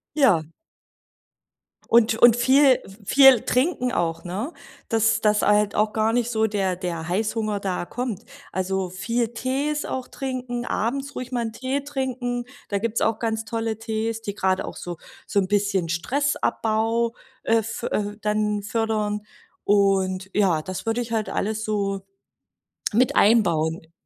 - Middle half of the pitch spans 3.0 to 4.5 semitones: Yes, average, 3.3 semitones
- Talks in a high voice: Yes, high, 220 Hz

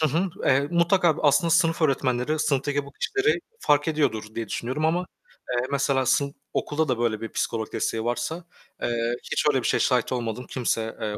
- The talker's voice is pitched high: No, medium, 140 Hz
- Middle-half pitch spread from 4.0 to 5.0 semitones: Yes, average, 4.7 semitones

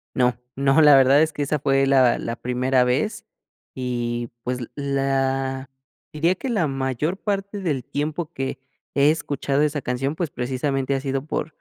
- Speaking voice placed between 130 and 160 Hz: Yes, low, 135 Hz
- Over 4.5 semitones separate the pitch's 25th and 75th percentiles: No, average, 2.7 semitones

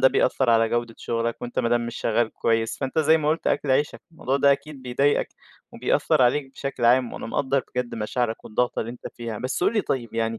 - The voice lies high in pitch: No, low, 125 Hz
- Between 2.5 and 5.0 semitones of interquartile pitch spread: Yes, average, 2.8 semitones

